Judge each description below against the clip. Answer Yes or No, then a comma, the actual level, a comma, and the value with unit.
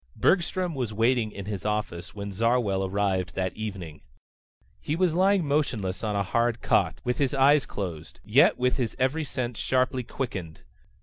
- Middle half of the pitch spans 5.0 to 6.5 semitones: Yes, average, 5.3 semitones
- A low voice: Yes, low, 115 Hz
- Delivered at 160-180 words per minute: Yes, average, 165 wpm